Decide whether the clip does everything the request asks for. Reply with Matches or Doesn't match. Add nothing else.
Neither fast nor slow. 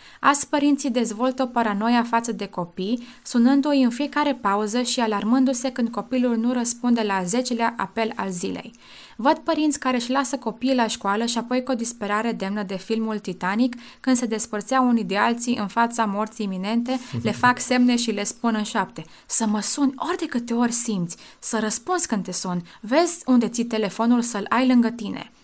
Doesn't match